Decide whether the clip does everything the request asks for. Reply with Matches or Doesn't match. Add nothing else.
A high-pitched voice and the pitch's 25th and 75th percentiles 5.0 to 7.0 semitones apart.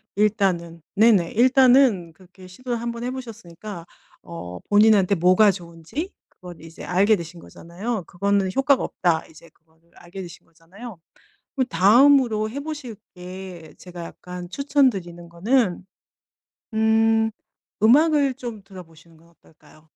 Matches